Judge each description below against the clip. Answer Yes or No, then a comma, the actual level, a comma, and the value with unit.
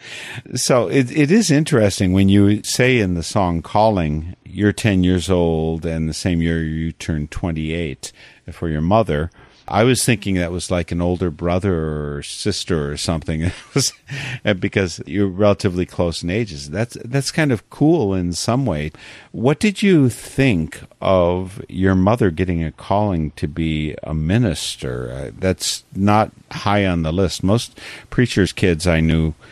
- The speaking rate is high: No, average, 160 wpm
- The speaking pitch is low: Yes, very low, 95 Hz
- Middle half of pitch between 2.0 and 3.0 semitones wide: No, average, 5.1 semitones